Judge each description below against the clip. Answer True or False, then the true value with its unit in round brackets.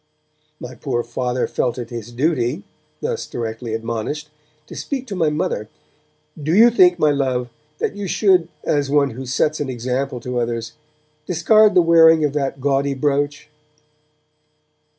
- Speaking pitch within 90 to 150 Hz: True (140 Hz)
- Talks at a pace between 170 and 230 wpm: False (155 wpm)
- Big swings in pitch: False (4.9 semitones)